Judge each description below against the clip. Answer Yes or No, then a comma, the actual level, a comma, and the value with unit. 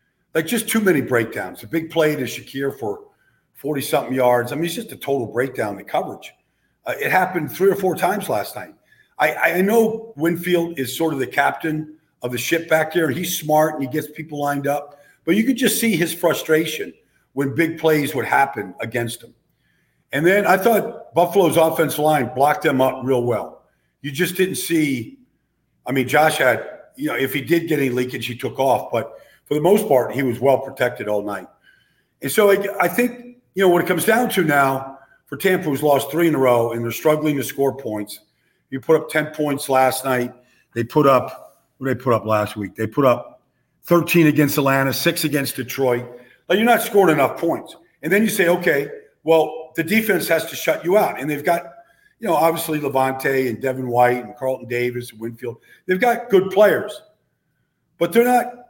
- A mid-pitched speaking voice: Yes, medium, 155 Hz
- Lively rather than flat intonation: No, average, 4.9 semitones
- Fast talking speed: Yes, fast, 210 wpm